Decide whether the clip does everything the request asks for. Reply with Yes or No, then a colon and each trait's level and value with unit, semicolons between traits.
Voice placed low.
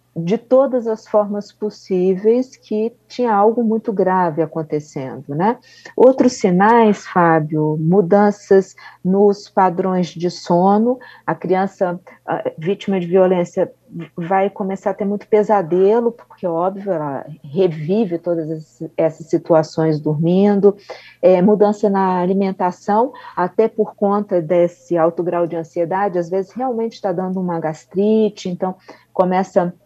No: high, 190 Hz